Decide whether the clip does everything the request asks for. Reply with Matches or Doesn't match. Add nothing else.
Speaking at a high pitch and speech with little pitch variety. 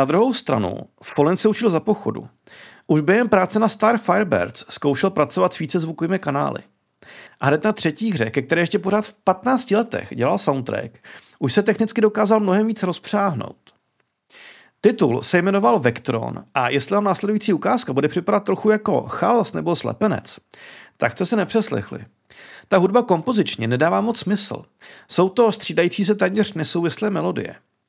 Doesn't match